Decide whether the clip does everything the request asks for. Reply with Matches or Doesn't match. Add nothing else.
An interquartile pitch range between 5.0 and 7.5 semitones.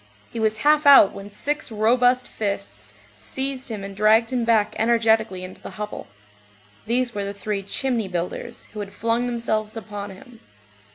Doesn't match